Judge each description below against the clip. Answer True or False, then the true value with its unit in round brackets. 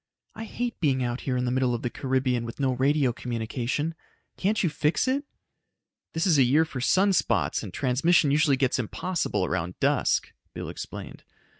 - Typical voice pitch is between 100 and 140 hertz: True (135 Hz)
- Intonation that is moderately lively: True (4.5 semitones)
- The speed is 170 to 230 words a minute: True (180 wpm)